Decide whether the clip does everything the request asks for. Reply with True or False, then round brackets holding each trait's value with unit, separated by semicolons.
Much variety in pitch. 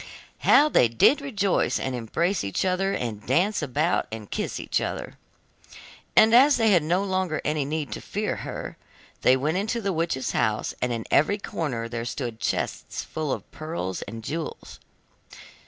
True (8.1 semitones)